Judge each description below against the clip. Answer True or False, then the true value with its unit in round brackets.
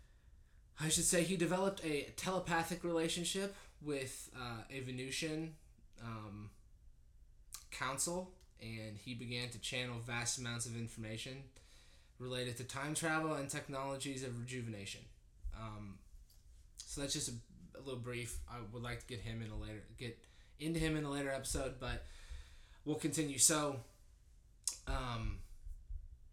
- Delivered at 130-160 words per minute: True (135 wpm)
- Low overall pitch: True (120 Hz)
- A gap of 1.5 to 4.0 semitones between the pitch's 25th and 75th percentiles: False (5.6 semitones)